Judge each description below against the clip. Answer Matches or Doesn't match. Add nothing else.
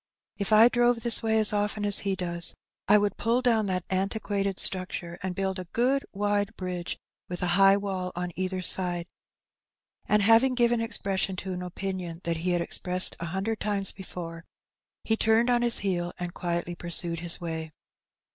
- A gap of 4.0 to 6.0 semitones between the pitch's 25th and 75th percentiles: Doesn't match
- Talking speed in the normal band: Matches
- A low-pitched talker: Doesn't match